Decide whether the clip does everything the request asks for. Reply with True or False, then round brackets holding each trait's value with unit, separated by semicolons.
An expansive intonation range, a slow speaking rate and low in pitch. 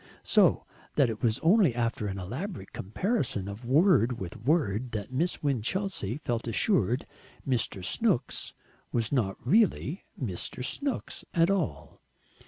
True (8.0 semitones; 130 wpm; 125 Hz)